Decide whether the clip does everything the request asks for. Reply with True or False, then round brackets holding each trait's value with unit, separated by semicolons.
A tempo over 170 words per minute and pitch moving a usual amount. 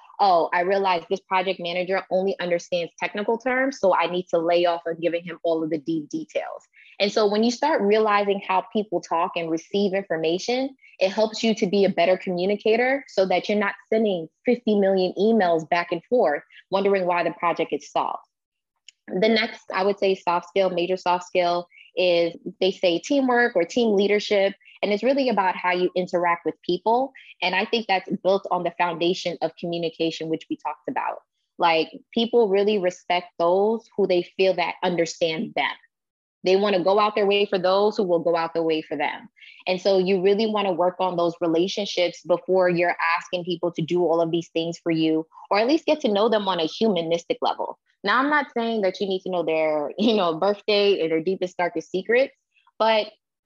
True (205 wpm; 3.4 semitones)